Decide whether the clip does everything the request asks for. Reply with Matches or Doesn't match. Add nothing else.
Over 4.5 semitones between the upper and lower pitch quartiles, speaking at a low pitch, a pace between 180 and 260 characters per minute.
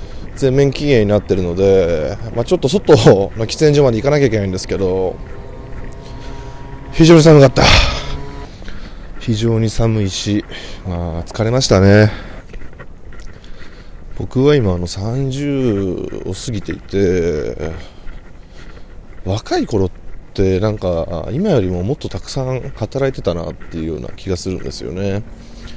Matches